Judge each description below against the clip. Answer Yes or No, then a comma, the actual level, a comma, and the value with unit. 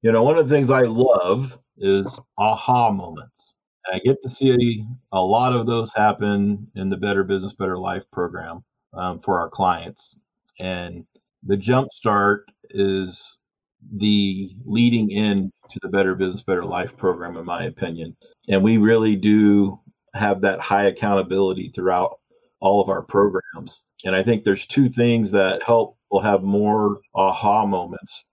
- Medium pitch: No, low, 100 Hz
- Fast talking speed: No, average, 160 wpm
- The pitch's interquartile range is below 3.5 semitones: Yes, average, 3.1 semitones